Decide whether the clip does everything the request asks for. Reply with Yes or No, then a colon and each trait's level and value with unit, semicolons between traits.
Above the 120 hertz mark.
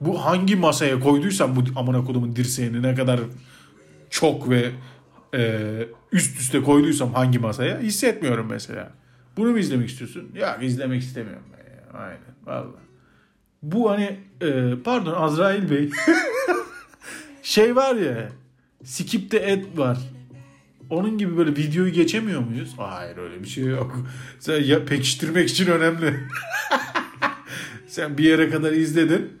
Yes: medium, 140 Hz